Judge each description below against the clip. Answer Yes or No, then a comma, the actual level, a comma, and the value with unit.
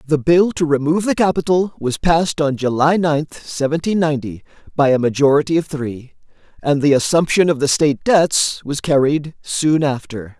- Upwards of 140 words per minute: Yes, average, 165 wpm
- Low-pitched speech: No, medium, 150 Hz